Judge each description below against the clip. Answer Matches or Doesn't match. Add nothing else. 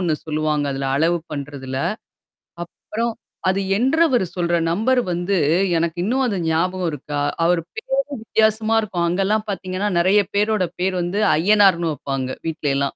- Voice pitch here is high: Doesn't match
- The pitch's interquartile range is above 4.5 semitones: Matches